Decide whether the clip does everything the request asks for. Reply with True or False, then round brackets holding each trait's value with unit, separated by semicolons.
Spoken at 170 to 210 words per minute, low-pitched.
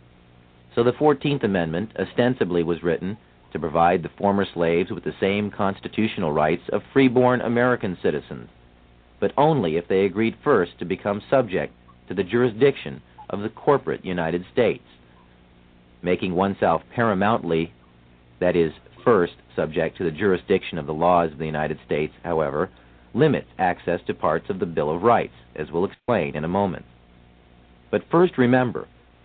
False (150 wpm; 85 Hz)